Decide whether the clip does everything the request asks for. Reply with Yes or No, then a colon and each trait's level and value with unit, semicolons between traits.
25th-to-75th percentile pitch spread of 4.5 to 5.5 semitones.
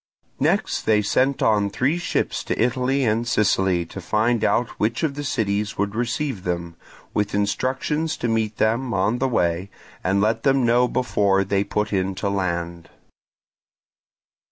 No: average, 4.1 semitones